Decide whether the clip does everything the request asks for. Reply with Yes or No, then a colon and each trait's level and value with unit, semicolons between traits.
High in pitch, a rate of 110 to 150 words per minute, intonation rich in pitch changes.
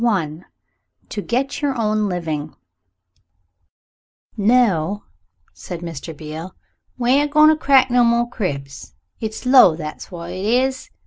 Yes: high, 210 Hz; average, 140 wpm; wide, 7.2 semitones